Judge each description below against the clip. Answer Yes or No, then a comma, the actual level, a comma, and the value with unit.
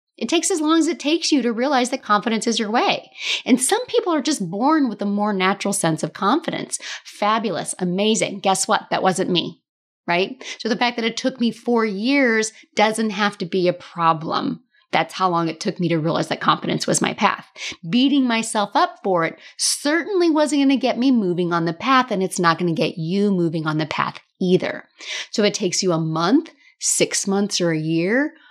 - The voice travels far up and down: Yes, wide, 6.4 semitones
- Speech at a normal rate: No, fast, 210 wpm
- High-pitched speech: Yes, high, 215 Hz